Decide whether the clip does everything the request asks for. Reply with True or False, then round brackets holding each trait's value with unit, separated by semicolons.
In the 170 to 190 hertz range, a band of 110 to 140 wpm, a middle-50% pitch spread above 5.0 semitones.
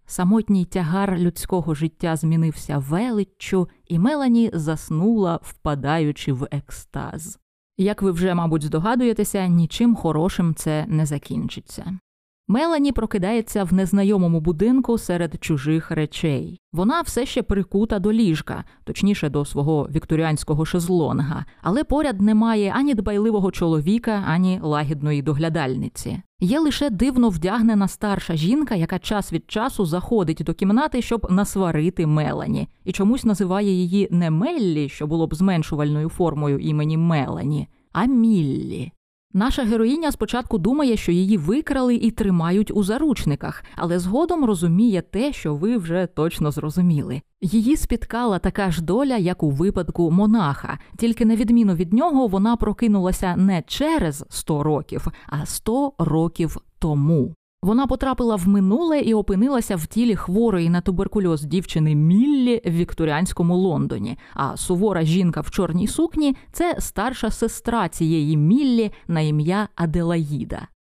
True (185 Hz; 130 wpm; 5.6 semitones)